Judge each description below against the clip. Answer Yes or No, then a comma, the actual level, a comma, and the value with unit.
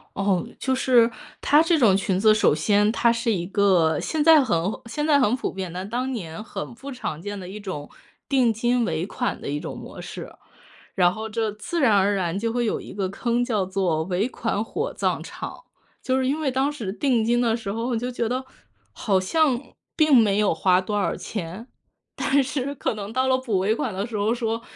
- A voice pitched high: Yes, high, 225 Hz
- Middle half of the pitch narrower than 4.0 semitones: No, average, 4.7 semitones